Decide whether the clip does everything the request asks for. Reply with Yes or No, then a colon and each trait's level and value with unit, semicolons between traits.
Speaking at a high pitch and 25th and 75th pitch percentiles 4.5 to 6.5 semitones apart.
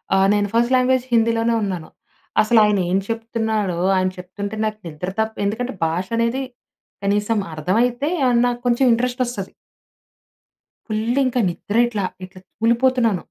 No: high, 225 Hz; average, 3.2 semitones